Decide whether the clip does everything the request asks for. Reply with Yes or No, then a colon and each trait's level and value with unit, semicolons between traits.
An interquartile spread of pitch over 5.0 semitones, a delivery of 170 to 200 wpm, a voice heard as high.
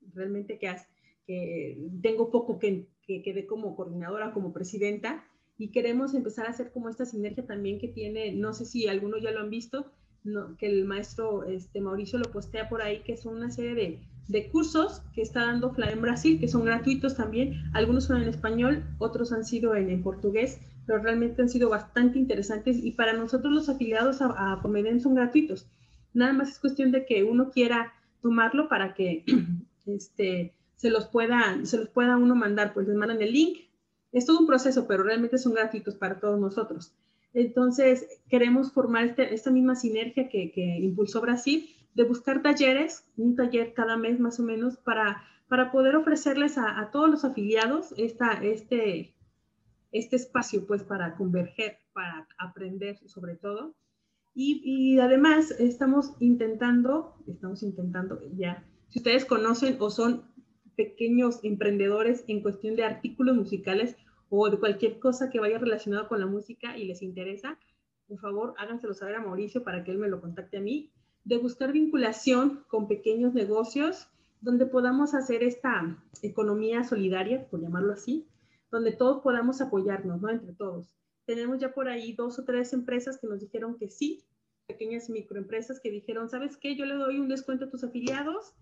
No: average, 3.7 semitones; average, 175 wpm; high, 230 Hz